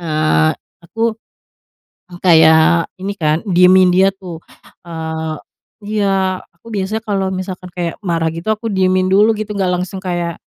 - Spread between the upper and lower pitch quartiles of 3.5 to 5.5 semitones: No, narrow, 2.5 semitones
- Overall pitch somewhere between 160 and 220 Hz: Yes, medium, 185 Hz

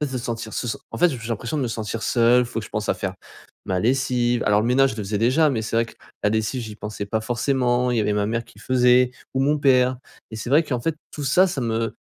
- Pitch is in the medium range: No, low, 120 Hz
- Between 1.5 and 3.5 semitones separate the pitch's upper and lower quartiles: Yes, average, 2.8 semitones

